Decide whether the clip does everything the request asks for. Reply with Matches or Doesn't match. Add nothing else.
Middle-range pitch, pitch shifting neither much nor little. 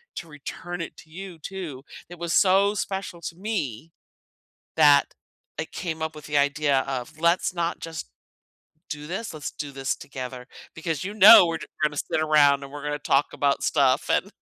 Matches